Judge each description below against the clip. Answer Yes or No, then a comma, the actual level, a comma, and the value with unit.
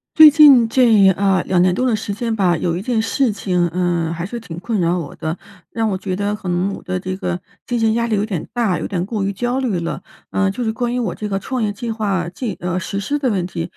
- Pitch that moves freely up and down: No, average, 4.3 semitones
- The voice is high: Yes, high, 200 Hz